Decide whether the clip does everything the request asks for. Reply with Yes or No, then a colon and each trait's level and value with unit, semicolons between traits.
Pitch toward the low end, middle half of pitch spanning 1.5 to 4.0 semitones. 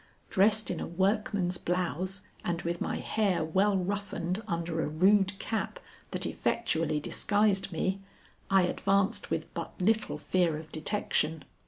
No: medium, 185 Hz; average, 3.2 semitones